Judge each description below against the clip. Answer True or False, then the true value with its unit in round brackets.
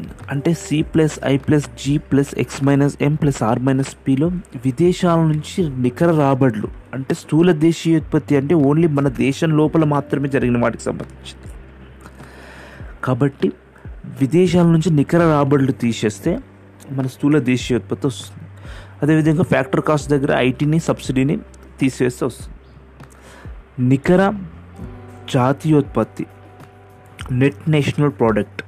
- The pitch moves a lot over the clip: False (5.0 semitones)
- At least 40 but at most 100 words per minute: False (115 wpm)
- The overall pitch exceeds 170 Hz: False (135 Hz)